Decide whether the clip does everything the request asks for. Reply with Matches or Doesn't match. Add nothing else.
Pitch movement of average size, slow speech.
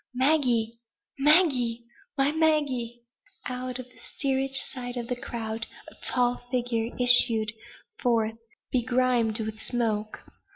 Doesn't match